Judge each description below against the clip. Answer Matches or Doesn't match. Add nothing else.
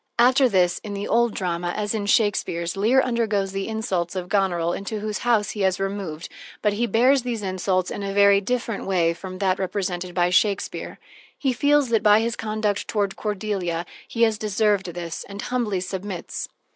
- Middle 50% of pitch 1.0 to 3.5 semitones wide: Matches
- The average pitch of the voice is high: Matches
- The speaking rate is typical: Matches